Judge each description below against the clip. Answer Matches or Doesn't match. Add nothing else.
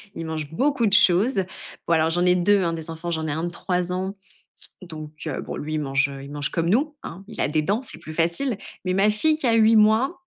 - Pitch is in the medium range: Matches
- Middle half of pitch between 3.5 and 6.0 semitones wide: Matches